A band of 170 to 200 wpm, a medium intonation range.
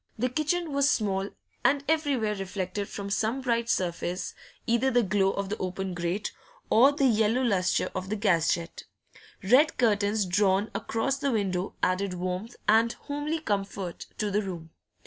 No: average, 160 wpm; average, 4.6 semitones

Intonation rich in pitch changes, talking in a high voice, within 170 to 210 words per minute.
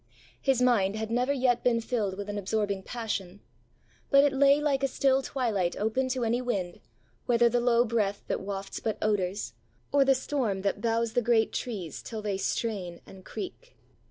No: average, 3.9 semitones; high, 230 Hz; average, 185 wpm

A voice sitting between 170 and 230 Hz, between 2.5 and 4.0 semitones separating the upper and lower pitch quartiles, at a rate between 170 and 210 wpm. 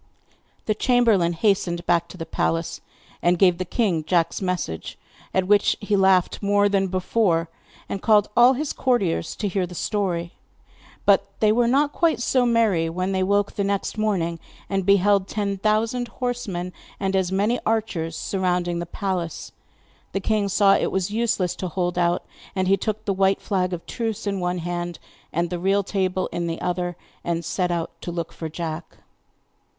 Yes: high, 190 Hz; average, 3.0 semitones; average, 175 wpm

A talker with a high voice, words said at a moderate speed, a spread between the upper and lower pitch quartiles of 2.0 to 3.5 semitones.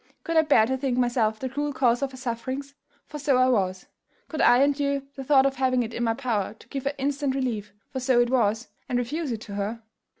No: very high, 255 Hz; fast, 235 wpm; average, 3.0 semitones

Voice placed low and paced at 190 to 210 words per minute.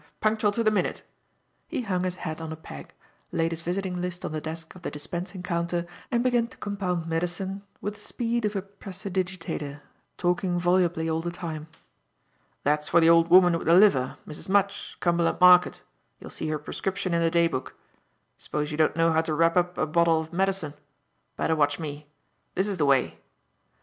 No: medium, 175 Hz; average, 195 wpm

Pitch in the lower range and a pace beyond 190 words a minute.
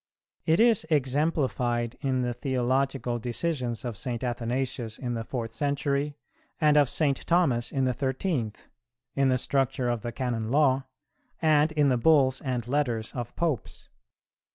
No: low, 130 Hz; average, 150 wpm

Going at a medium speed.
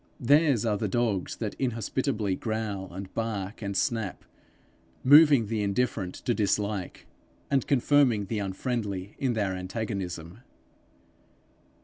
No: slow, 115 wpm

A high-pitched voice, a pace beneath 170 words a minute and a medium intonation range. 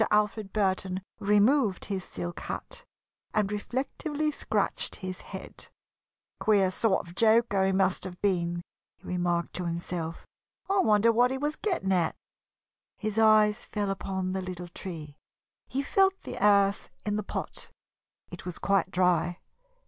Yes: high, 195 Hz; average, 145 wpm; average, 3.0 semitones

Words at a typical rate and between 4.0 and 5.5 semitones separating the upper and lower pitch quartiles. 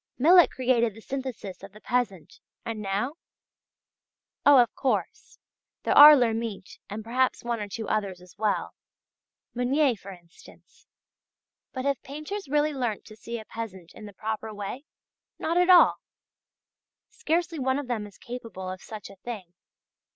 Yes: average, 155 wpm; average, 4.6 semitones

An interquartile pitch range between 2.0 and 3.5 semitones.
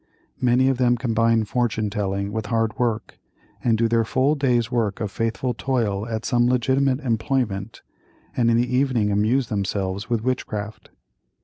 Yes: average, 2.8 semitones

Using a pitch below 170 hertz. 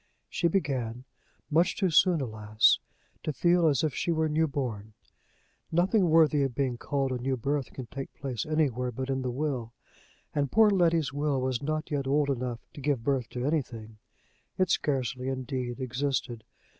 Yes: low, 135 Hz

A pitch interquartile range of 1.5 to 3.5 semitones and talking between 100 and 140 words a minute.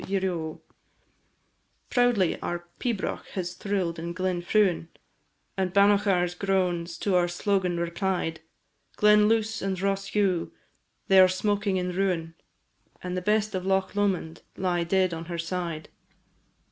Yes: narrow, 2.4 semitones; slow, 135 wpm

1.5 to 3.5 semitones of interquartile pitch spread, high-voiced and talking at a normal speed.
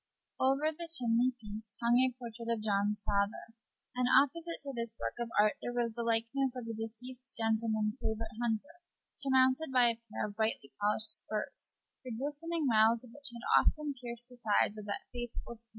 Yes: average, 2.8 semitones; high, 235 Hz; average, 185 wpm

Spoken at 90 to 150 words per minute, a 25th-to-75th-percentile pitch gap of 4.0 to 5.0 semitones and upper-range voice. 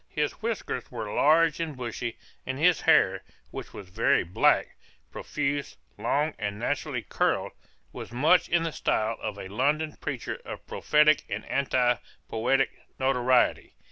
No: average, 140 wpm; average, 4.5 semitones; low, 135 Hz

